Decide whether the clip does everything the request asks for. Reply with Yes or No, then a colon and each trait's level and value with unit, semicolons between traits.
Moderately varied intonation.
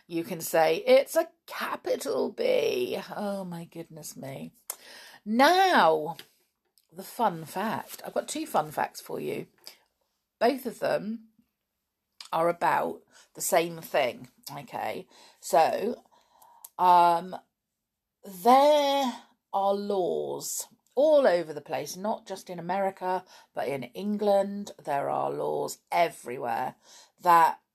No: wide, 9.0 semitones